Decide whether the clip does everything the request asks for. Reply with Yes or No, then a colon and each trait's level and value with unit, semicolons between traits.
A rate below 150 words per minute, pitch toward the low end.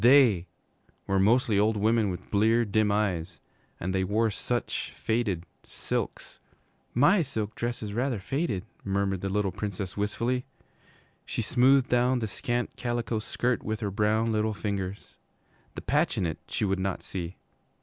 No: average, 155 wpm; low, 105 Hz